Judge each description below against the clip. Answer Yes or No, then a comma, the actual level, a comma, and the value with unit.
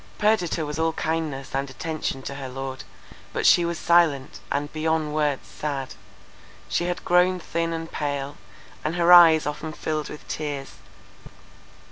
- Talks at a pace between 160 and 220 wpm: No, average, 150 wpm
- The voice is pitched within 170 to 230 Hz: No, medium, 155 Hz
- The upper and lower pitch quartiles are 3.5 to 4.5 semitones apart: No, average, 2.9 semitones